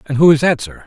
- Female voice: No, male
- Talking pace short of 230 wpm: No, fast, 345 wpm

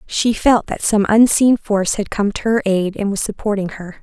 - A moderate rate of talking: No, fast, 225 wpm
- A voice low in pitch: No, high, 205 Hz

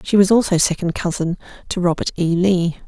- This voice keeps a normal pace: Yes, average, 190 wpm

